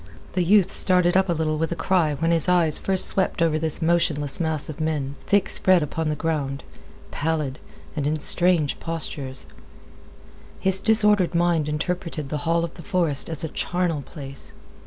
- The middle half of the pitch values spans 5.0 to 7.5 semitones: No, average, 2.9 semitones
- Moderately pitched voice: Yes, medium, 165 Hz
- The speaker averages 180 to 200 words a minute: No, average, 170 wpm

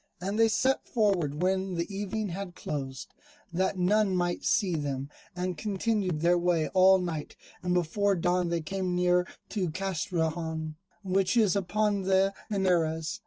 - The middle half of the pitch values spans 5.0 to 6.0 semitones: No, narrow, 2.6 semitones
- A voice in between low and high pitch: Yes, medium, 180 Hz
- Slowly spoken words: No, average, 150 wpm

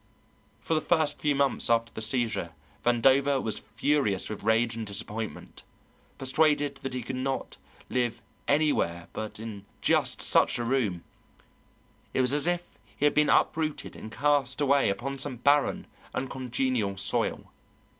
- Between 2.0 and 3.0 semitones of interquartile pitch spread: No, average, 4.2 semitones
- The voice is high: No, low, 130 Hz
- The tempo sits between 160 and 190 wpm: No, average, 145 wpm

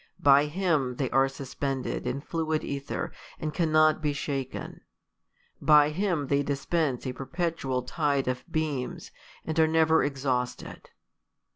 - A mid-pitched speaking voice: Yes, medium, 145 Hz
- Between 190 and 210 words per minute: No, average, 140 wpm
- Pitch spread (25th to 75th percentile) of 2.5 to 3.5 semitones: Yes, average, 2.8 semitones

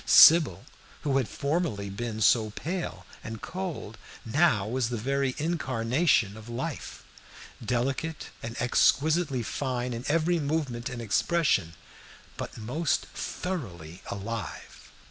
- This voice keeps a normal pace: No, slow, 115 wpm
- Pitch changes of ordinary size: No, wide, 6.0 semitones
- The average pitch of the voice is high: No, low, 125 Hz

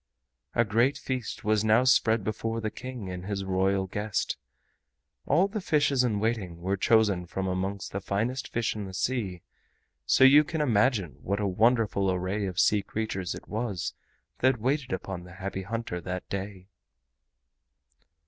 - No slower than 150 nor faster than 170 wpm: Yes, average, 160 wpm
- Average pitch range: Yes, average, 3.9 semitones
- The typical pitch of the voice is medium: No, low, 105 Hz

